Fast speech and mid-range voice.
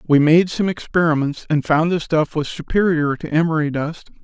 No: average, 185 wpm; medium, 160 Hz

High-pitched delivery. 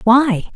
Yes: high, 240 Hz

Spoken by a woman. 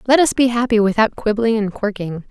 Yes: female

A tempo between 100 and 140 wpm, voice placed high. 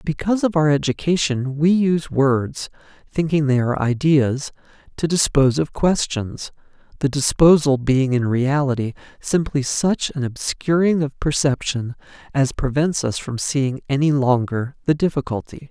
No: slow, 135 wpm; medium, 140 Hz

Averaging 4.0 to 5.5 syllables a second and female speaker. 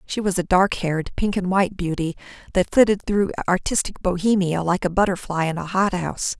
No: 5.7 syllables/s; female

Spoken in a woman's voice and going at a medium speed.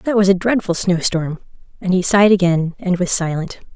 Yes: female; average, 190 wpm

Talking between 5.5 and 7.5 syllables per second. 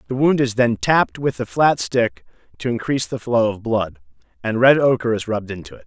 Yes: 5.7 syllables/s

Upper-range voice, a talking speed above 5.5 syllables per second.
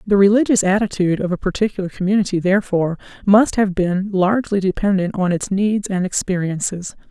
Yes: high, 195 Hz; 5.9 syllables/s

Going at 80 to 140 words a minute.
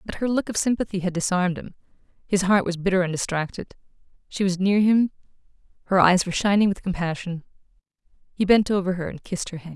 No: average, 190 wpm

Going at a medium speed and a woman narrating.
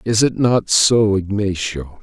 No: average, 150 wpm; male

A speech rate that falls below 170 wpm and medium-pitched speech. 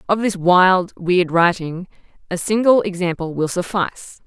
Yes: average, 140 wpm; medium, 180 Hz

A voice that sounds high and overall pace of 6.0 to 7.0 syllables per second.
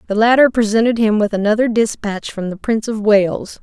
No: high, 215 Hz; 5.5 syllables/s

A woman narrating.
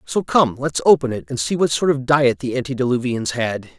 No: male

